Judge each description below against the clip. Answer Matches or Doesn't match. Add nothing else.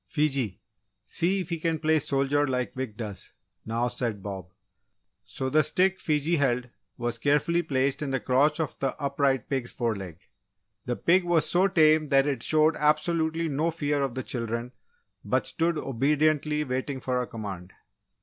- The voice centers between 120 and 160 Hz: Matches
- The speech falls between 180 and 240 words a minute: Doesn't match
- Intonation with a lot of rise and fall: Doesn't match